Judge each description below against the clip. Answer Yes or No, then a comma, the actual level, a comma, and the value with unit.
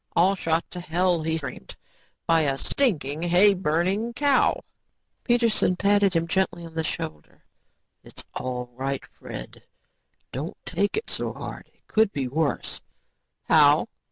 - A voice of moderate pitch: Yes, medium, 170 Hz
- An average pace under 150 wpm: Yes, slow, 135 wpm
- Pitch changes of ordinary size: Yes, average, 5.0 semitones